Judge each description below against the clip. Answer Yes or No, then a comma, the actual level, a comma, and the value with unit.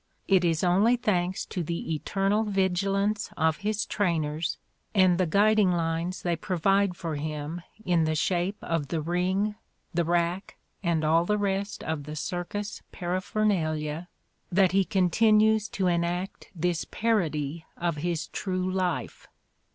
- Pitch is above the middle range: No, medium, 180 Hz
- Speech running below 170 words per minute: Yes, average, 140 wpm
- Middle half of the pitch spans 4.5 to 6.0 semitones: No, average, 3.1 semitones